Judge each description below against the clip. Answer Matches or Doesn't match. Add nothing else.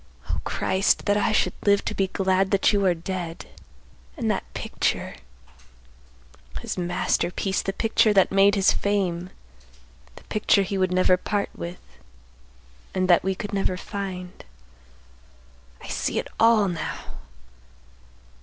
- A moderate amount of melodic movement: Doesn't match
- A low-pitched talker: Doesn't match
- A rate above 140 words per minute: Doesn't match